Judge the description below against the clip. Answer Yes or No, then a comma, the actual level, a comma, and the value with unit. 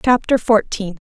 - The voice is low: No, high, 215 Hz